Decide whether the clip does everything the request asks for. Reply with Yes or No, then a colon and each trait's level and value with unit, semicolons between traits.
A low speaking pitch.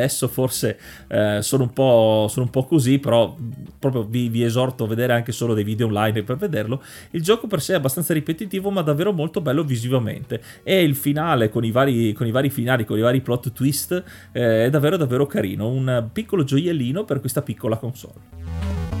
Yes: low, 125 Hz